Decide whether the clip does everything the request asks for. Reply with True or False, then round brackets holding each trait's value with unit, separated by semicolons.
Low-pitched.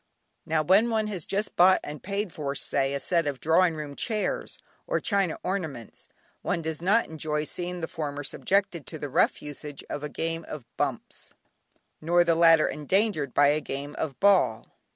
False (160 Hz)